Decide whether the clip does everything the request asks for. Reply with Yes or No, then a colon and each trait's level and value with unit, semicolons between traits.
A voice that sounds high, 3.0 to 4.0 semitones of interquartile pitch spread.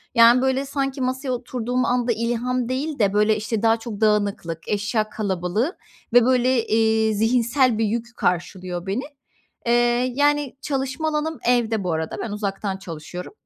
Yes: high, 230 Hz; average, 3.4 semitones